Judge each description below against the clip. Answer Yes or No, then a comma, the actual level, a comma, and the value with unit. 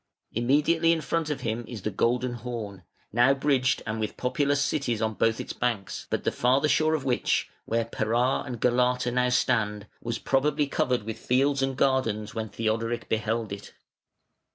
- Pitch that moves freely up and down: No, average, 3.3 semitones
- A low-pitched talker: Yes, low, 125 Hz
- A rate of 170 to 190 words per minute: Yes, average, 175 wpm